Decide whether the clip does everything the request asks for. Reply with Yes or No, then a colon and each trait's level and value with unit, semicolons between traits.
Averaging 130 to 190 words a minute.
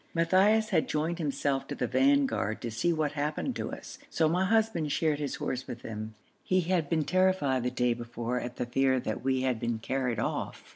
No: fast, 205 wpm